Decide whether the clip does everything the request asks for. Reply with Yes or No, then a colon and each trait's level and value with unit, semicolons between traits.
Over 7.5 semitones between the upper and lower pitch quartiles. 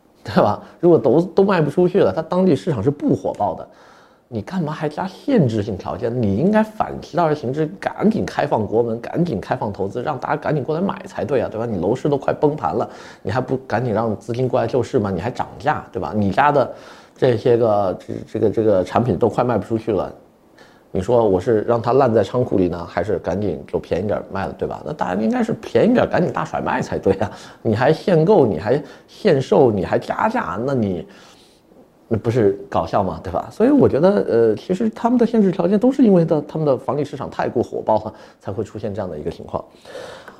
Yes: wide, 8.3 semitones